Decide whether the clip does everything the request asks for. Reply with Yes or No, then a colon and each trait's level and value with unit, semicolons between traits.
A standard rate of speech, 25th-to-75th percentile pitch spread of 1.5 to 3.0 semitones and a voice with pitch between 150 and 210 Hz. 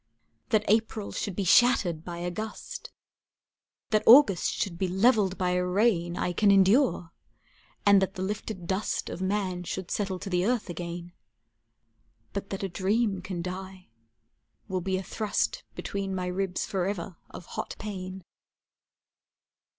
Yes: average, 150 wpm; narrow, 2.4 semitones; high, 190 Hz